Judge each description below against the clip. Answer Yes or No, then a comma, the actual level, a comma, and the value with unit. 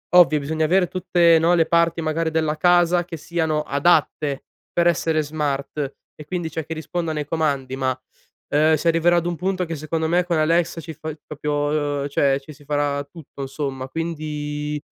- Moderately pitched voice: Yes, medium, 155 Hz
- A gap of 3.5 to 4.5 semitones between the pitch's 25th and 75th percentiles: No, narrow, 2.4 semitones